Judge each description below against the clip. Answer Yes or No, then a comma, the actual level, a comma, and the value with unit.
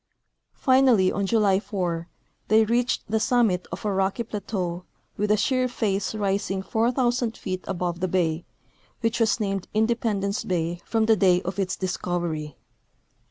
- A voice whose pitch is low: No, high, 200 Hz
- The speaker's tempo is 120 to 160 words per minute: Yes, average, 150 wpm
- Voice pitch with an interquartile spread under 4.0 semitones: Yes, average, 3.4 semitones